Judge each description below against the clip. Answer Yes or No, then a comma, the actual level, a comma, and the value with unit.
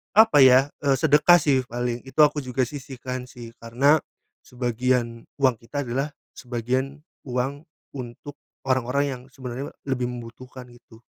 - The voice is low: Yes, low, 130 Hz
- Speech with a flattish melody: Yes, narrow, 2.3 semitones